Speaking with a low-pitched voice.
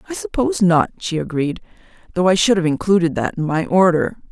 No: medium, 180 Hz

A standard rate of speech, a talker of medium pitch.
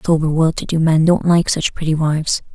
No: fast, 235 wpm; medium, 160 Hz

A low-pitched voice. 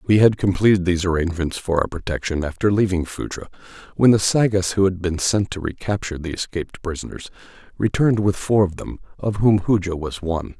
Yes: very low, 95 Hz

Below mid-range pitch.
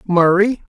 No: high, 190 Hz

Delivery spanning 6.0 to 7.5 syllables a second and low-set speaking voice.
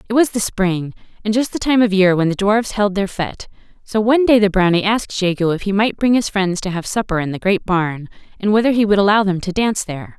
No: 6.1 syllables/s; high, 200 Hz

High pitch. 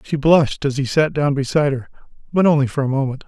No: medium, 140 Hz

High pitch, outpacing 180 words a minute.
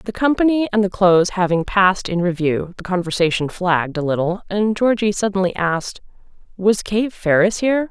No: high, 195 Hz; average, 165 wpm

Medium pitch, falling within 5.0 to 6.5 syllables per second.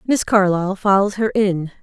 No: high, 205 Hz; 5.7 syllables/s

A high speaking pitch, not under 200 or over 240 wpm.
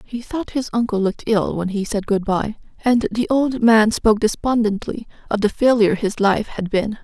Yes: high, 220 Hz; fast, 205 wpm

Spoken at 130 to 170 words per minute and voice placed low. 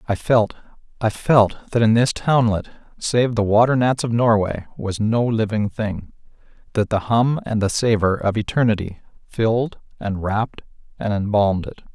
Yes: average, 160 wpm; low, 110 Hz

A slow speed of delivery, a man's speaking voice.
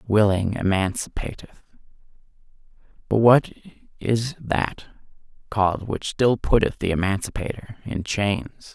Yes: slow, 95 wpm; male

